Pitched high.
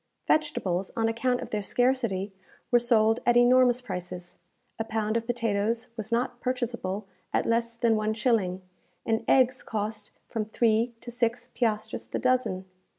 Yes: high, 230 Hz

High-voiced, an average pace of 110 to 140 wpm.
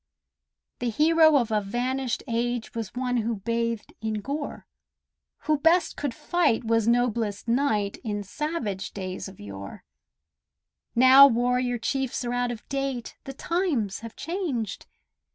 Yes: high, 240 Hz; slow, 135 wpm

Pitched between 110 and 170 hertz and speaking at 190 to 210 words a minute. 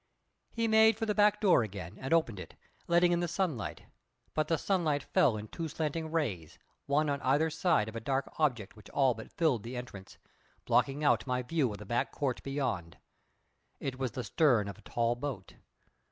Yes: medium, 140 Hz; average, 195 wpm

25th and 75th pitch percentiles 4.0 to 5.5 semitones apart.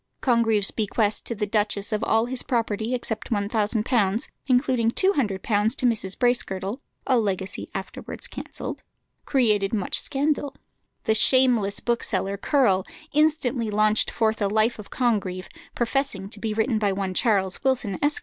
No: average, 3.4 semitones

